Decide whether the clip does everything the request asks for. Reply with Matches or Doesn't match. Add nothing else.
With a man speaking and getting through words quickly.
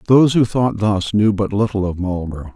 Matches